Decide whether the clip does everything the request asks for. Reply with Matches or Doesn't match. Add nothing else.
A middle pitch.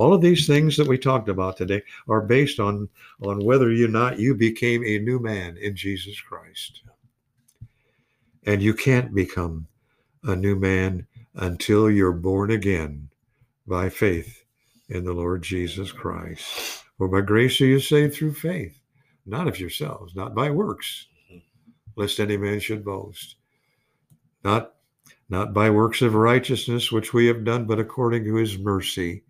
Doesn't match